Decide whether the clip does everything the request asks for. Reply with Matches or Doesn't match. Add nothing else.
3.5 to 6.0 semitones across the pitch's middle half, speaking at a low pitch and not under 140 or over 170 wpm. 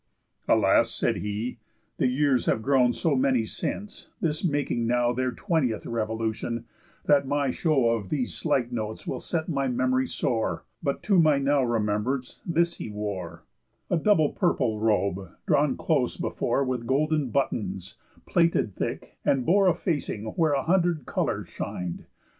Matches